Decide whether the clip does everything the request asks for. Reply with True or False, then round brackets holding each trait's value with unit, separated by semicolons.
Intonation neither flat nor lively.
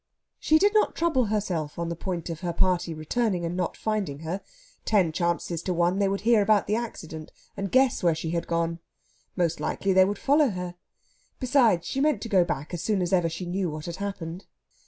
True (4.0 semitones)